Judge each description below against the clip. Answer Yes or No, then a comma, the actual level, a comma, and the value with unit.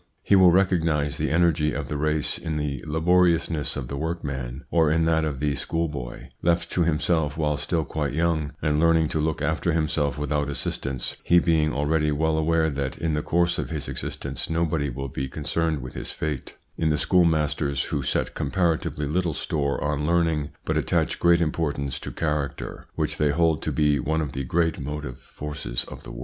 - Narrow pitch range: Yes, narrow, 2.3 semitones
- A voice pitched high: No, very low, 75 Hz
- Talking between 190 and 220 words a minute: Yes, average, 195 wpm